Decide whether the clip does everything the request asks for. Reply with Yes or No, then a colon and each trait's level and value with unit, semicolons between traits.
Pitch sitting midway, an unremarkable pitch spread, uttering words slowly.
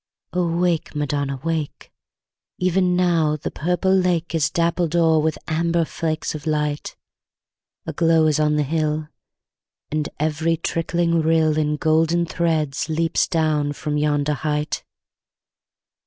No: medium, 160 Hz; narrow, 1.8 semitones; slow, 130 wpm